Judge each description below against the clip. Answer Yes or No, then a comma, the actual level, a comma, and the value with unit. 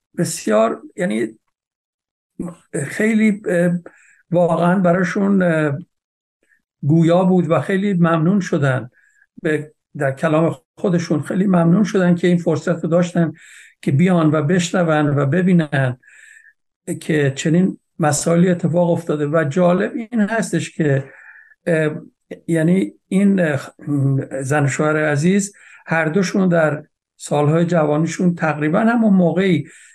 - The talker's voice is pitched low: No, medium, 170 Hz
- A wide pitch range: No, average, 3.2 semitones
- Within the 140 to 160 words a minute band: No, slow, 100 wpm